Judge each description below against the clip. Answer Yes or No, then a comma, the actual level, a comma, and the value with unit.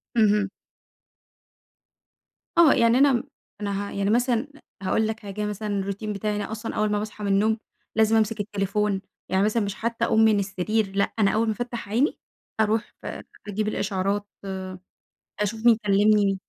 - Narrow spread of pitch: Yes, narrow, 1.7 semitones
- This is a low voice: No, high, 210 Hz